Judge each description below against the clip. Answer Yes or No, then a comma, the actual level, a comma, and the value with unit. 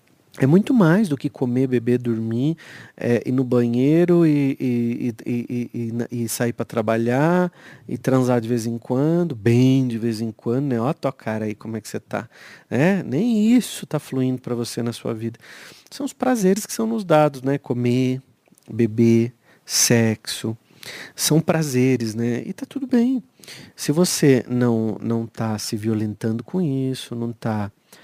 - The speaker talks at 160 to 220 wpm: Yes, average, 175 wpm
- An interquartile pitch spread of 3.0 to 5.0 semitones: Yes, average, 4.7 semitones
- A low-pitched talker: Yes, low, 125 Hz